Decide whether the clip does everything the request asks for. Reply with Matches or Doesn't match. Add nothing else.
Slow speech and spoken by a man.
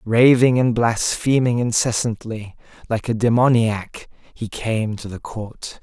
Matches